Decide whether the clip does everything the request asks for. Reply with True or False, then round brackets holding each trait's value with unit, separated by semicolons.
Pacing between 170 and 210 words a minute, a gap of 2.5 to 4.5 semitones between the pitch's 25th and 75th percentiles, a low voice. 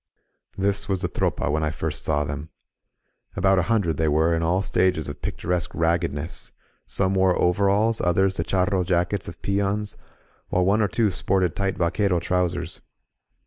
True (175 wpm; 2.8 semitones; 90 Hz)